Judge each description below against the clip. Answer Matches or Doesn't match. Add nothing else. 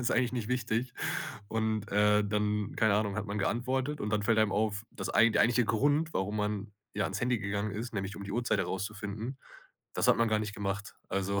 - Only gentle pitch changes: Matches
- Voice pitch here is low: Matches